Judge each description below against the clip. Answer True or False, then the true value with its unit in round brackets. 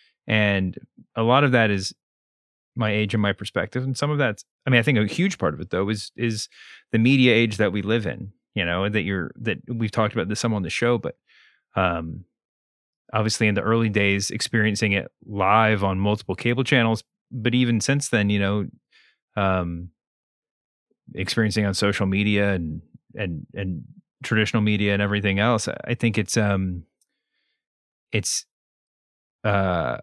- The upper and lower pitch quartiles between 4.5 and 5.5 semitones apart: False (2.8 semitones)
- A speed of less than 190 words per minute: True (170 wpm)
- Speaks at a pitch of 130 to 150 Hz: False (105 Hz)